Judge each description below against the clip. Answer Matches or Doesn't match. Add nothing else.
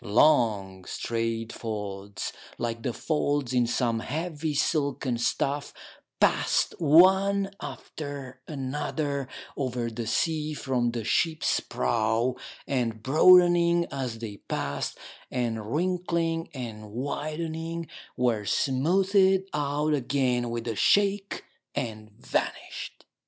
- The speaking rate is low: Matches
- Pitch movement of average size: Doesn't match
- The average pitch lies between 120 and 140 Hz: Matches